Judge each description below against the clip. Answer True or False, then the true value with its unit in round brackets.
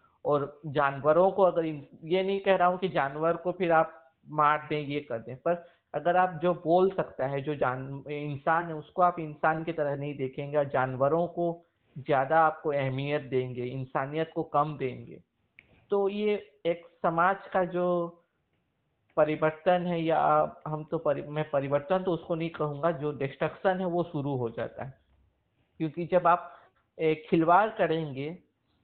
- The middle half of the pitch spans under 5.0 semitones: True (3.3 semitones)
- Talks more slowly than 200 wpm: True (165 wpm)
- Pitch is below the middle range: False (160 Hz)